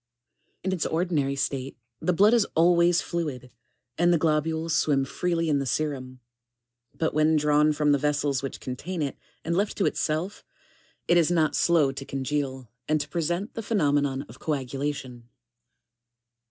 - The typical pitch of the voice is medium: Yes, medium, 150 Hz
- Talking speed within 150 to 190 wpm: Yes, average, 165 wpm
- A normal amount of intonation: Yes, average, 3.7 semitones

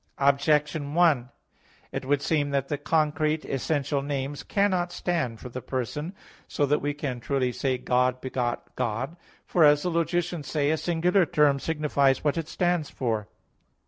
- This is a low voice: No, medium, 145 Hz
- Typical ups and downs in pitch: Yes, average, 3.4 semitones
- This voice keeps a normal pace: Yes, average, 160 wpm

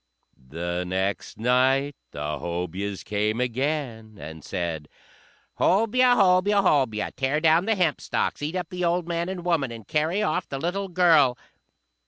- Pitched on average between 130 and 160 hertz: Yes, medium, 140 Hz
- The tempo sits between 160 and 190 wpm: No, average, 145 wpm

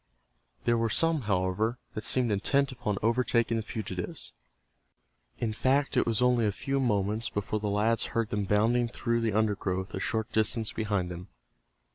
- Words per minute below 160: No, average, 165 wpm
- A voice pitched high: No, low, 110 Hz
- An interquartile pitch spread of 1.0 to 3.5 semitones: Yes, narrow, 2.4 semitones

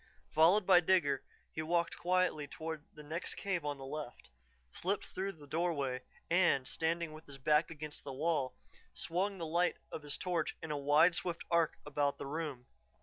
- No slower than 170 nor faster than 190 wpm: Yes, average, 180 wpm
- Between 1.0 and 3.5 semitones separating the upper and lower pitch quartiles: Yes, average, 2.9 semitones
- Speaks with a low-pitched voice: No, medium, 160 Hz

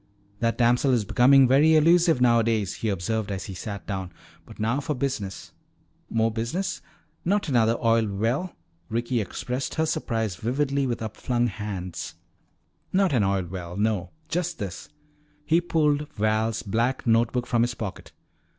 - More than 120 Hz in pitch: No, low, 115 Hz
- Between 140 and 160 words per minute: Yes, average, 155 wpm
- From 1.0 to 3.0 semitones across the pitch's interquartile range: No, average, 4.6 semitones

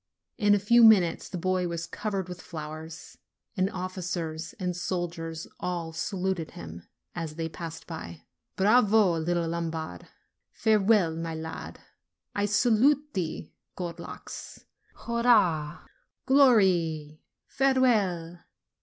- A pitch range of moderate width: Yes, average, 4.0 semitones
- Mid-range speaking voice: Yes, medium, 175 Hz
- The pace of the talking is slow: Yes, slow, 110 wpm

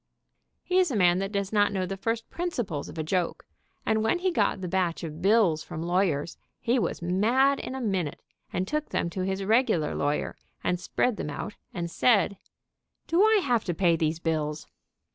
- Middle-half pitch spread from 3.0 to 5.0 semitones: No, wide, 5.4 semitones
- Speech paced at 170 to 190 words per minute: No, average, 200 wpm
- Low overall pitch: No, high, 195 Hz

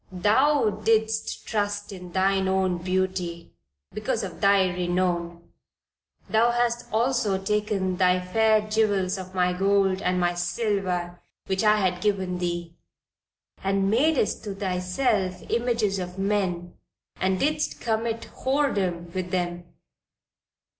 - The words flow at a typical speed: No, slow, 120 wpm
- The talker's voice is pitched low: No, high, 195 Hz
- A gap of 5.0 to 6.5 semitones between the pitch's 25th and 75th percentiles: No, average, 3.0 semitones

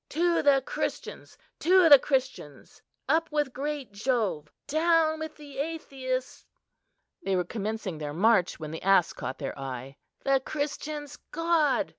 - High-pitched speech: Yes, very high, 270 Hz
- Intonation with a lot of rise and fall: Yes, wide, 7.7 semitones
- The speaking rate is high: No, average, 140 wpm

